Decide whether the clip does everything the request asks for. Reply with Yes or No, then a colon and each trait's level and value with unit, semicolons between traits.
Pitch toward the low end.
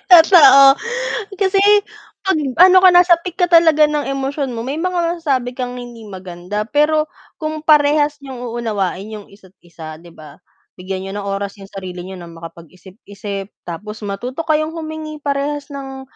No: very high, 260 Hz